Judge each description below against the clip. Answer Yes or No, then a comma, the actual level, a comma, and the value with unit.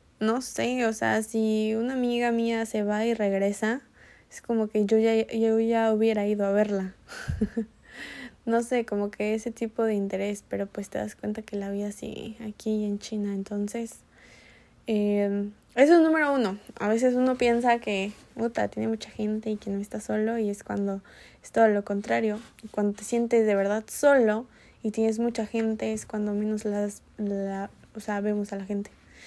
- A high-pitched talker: Yes, high, 215 Hz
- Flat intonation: Yes, narrow, 1.9 semitones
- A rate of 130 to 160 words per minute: No, average, 185 wpm